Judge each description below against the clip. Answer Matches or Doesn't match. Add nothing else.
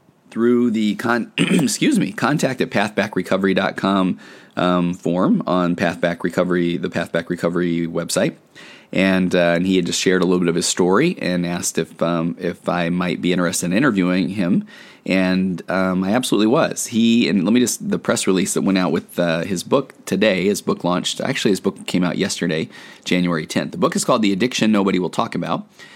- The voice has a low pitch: Matches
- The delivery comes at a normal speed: Matches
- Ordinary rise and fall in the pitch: Doesn't match